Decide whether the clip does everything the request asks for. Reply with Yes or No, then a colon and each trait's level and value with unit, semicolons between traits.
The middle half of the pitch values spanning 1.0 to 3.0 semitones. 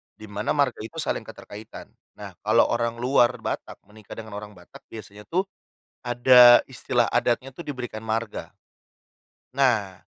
Yes: average, 2.7 semitones